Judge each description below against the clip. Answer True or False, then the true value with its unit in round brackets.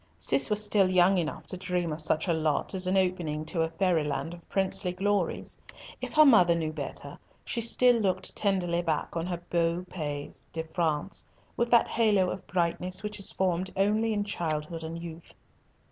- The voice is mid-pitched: True (180 Hz)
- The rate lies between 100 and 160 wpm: False (190 wpm)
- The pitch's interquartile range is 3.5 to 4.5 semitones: False (3.1 semitones)